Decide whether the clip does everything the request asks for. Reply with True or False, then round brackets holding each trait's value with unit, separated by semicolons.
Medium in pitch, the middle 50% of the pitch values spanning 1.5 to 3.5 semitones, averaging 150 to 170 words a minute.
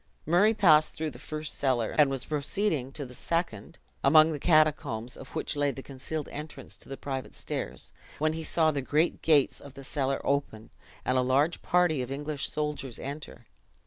False (145 Hz; 2.7 semitones; 185 wpm)